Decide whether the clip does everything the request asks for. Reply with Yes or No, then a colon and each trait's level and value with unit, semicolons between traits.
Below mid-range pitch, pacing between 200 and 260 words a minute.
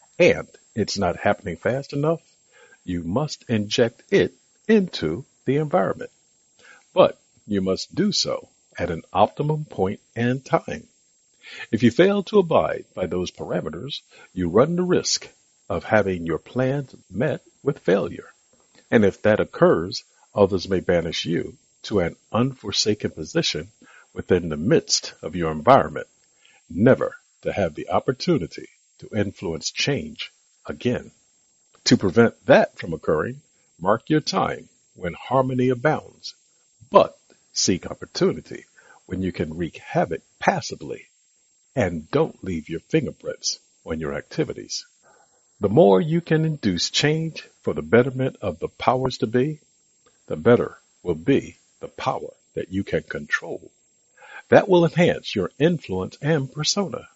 No: low, 130 Hz; slow, 135 wpm